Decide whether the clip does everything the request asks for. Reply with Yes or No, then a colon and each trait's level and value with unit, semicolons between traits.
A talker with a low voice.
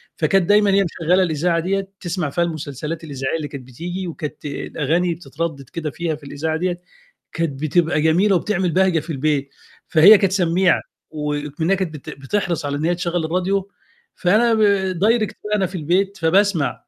No: medium, 170 Hz